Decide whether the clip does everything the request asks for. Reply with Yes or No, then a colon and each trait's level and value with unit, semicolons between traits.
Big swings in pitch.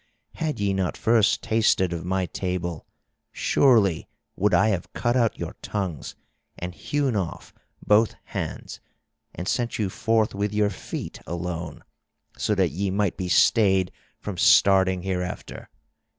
No: average, 3.1 semitones